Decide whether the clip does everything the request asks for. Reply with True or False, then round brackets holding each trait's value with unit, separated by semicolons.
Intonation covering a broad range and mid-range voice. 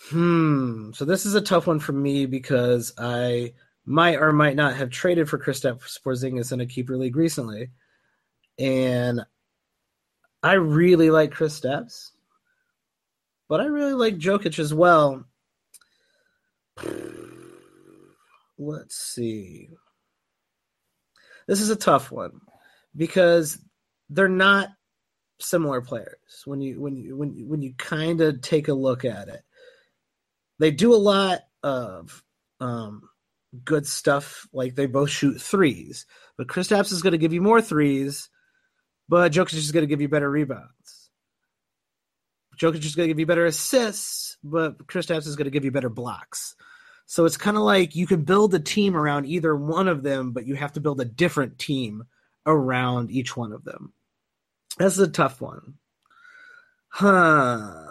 True (6.1 semitones; 155 Hz)